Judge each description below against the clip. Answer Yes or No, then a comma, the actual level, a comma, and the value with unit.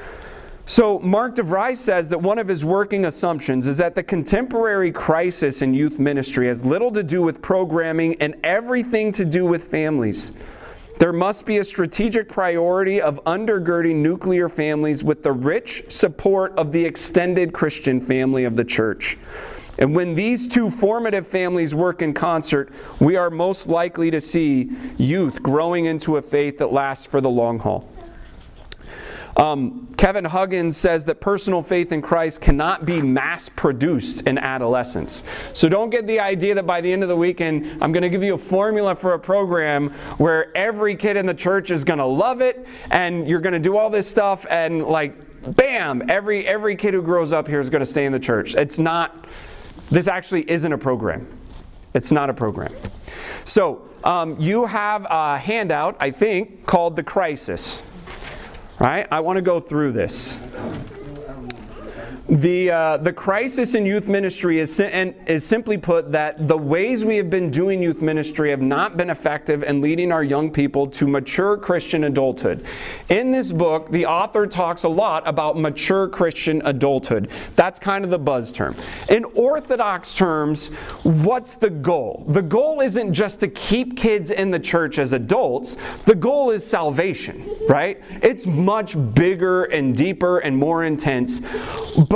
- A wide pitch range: No, average, 4.6 semitones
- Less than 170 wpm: No, average, 175 wpm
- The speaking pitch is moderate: Yes, medium, 170 Hz